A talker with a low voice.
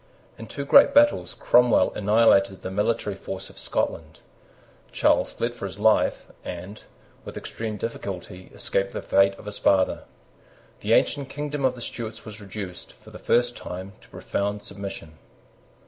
Yes: low, 105 Hz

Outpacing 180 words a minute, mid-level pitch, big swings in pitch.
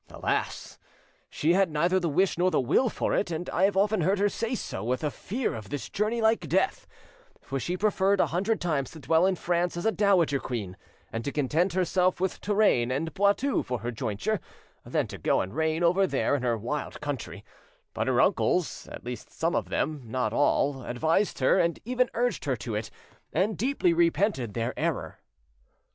Yes: average, 200 wpm; medium, 170 Hz; wide, 6.6 semitones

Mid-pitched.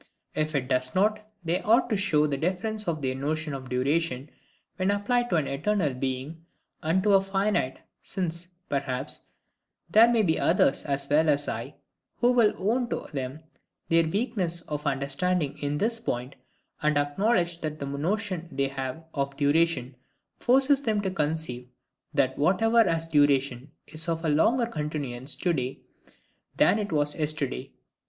Yes: medium, 160 Hz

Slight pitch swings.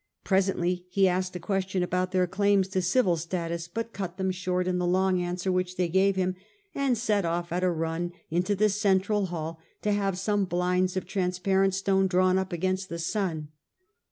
Yes: narrow, 1.4 semitones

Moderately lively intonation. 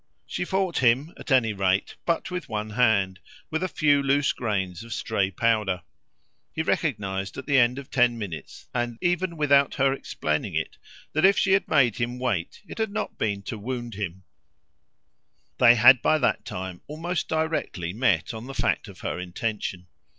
No: wide, 6.3 semitones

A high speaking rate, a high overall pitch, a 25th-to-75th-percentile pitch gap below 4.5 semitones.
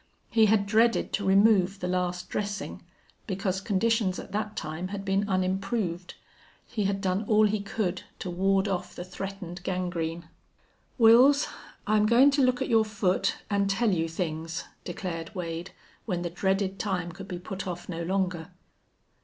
No: average, 160 wpm; high, 195 Hz; average, 2.8 semitones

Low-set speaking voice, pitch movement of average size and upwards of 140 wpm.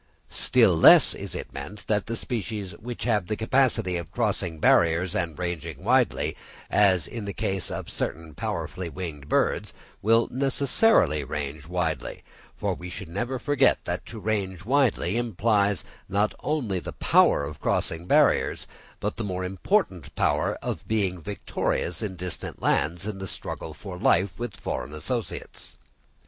Yes: very low, 95 Hz; average, 4.5 semitones; average, 150 wpm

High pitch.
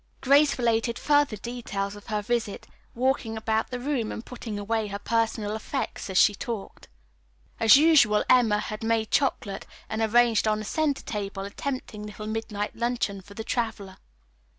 Yes: high, 225 Hz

